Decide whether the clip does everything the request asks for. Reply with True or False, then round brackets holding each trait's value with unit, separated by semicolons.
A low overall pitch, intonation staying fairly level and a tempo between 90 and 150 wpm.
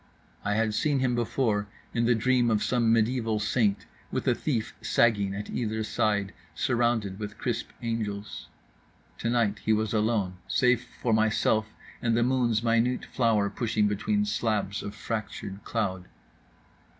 True (110 Hz; 2.3 semitones; 145 wpm)